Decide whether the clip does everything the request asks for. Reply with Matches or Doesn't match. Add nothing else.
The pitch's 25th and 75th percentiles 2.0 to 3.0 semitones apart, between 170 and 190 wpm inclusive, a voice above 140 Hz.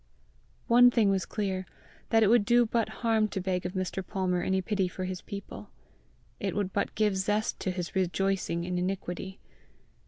Matches